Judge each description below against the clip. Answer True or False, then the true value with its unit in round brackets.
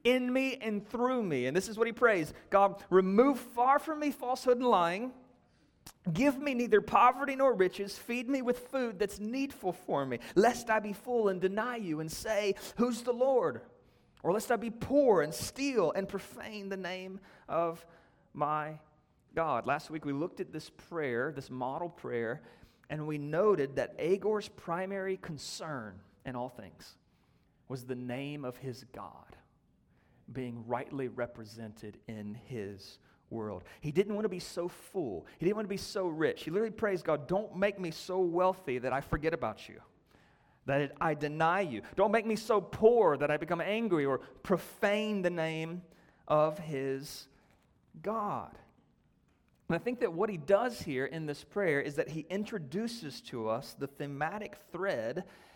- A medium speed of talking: True (170 wpm)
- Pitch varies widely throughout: True (6.9 semitones)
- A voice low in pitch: False (185 Hz)